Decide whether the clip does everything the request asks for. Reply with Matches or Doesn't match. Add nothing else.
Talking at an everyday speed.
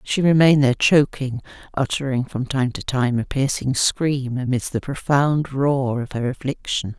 Matches